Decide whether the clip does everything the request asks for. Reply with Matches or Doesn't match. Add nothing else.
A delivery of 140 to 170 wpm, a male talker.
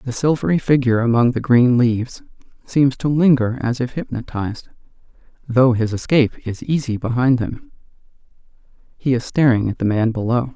Matches